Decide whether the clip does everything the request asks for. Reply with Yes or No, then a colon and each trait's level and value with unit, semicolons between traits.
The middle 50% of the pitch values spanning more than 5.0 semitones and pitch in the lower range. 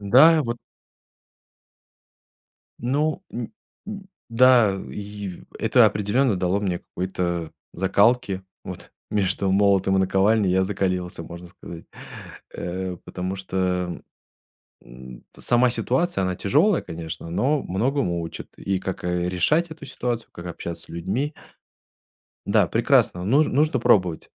Yes: wide, 5.4 semitones; very low, 95 Hz